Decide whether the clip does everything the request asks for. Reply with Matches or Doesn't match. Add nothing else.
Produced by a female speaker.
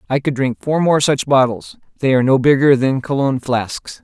Doesn't match